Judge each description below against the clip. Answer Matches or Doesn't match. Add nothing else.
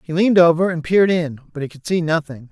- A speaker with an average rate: Doesn't match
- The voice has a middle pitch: Matches